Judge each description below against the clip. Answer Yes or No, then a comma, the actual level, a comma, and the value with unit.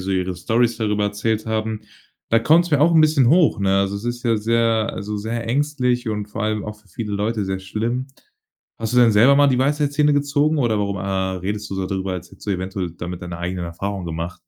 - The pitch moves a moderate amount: Yes, average, 4.1 semitones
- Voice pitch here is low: Yes, low, 110 Hz